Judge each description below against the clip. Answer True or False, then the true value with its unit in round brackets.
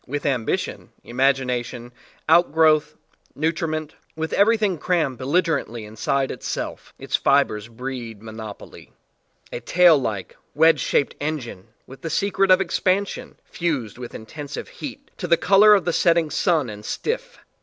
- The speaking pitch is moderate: True (155 Hz)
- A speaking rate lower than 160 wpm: True (145 wpm)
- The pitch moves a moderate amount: False (6.2 semitones)